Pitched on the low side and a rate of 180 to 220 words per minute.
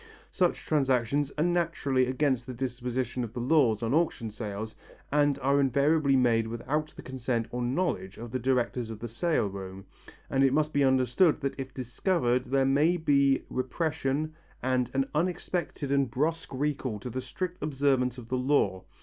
No: low, 130 Hz; average, 170 wpm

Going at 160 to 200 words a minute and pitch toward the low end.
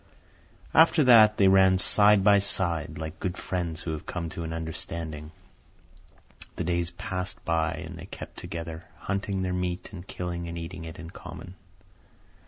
Yes: average, 165 wpm; very low, 90 Hz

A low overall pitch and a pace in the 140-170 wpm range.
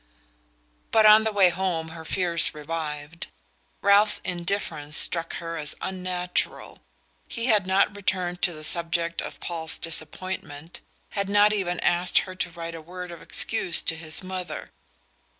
No: medium, 175 Hz; average, 150 wpm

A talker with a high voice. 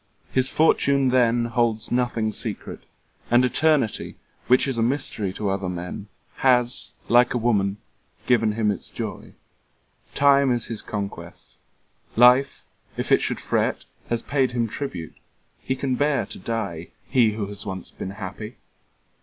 No: low, 120 Hz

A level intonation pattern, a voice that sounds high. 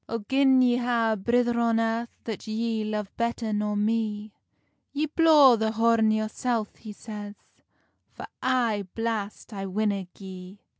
Yes: narrow, 2.1 semitones; high, 225 Hz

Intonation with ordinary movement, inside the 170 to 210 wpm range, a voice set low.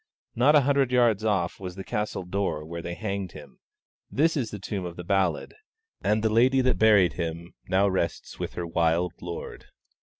Yes: average, 4.3 semitones; average, 190 wpm; very low, 95 Hz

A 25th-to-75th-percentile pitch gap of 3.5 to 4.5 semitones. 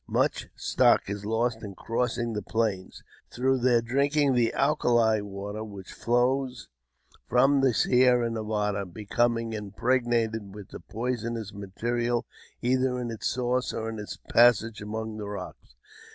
No: average, 2.7 semitones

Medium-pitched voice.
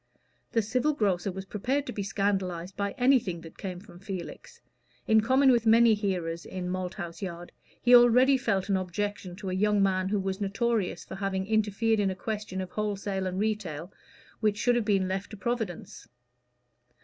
No: high, 200 Hz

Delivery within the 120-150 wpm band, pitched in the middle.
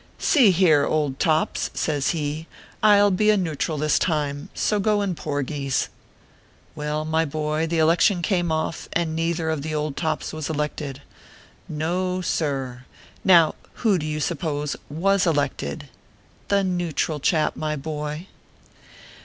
Yes: average, 145 wpm; medium, 155 Hz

